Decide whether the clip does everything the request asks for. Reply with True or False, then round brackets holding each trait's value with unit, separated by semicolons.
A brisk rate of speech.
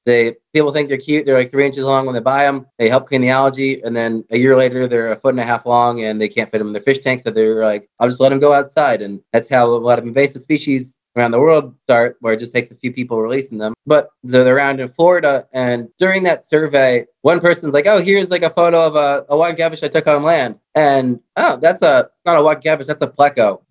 True (275 wpm)